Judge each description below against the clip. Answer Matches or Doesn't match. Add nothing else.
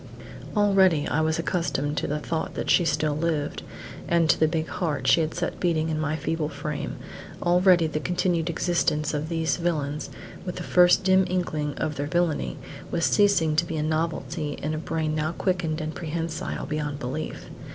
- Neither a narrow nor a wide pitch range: Doesn't match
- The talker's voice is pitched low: Doesn't match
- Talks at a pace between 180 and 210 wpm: Matches